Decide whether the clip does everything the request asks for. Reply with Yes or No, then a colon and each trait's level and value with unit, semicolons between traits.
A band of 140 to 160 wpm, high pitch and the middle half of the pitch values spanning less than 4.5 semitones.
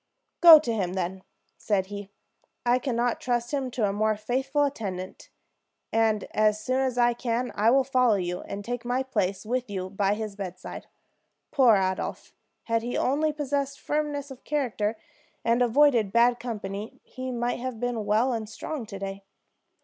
No: average, 170 wpm; high, 235 Hz; average, 3.9 semitones